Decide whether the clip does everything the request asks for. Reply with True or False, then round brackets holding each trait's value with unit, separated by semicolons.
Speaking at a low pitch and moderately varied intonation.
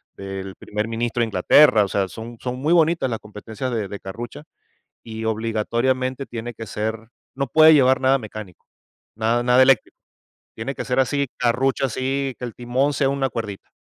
True (120 Hz; 3.2 semitones)